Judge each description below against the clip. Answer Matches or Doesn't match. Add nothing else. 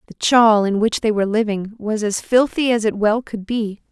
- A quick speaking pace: Matches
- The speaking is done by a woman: Matches